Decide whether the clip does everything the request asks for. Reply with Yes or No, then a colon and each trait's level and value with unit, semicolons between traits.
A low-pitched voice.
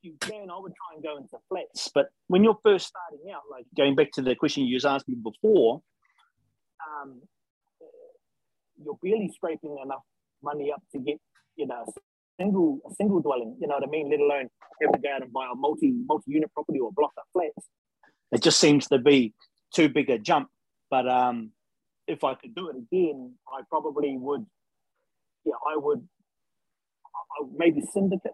No: medium, 155 Hz